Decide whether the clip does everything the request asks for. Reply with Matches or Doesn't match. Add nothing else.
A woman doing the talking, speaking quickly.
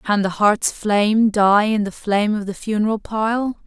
Doesn't match